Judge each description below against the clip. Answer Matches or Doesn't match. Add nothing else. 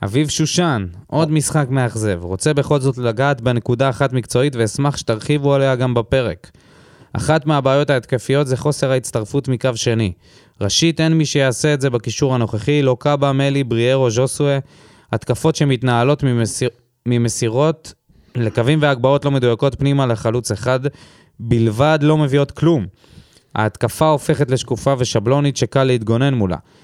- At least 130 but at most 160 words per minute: Matches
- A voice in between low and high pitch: Doesn't match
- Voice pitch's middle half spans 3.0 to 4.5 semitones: Matches